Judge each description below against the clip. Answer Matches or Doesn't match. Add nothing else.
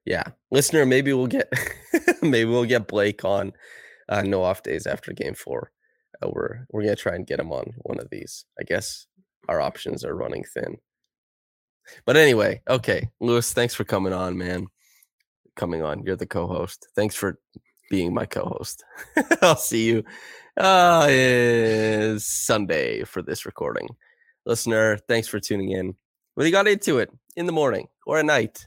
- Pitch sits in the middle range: Doesn't match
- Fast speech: Doesn't match